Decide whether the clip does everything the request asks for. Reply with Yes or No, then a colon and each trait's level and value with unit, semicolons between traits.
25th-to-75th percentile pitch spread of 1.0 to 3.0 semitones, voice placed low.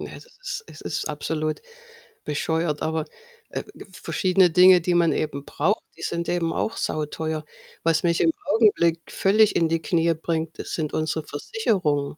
No: average, 2.7 semitones; medium, 165 Hz